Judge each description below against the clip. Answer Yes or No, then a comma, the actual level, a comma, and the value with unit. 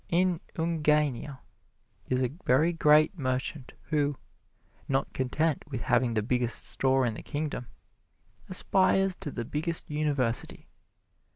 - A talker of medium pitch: Yes, medium, 145 Hz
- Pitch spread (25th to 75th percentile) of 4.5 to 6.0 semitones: No, average, 3.8 semitones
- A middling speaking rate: No, slow, 120 wpm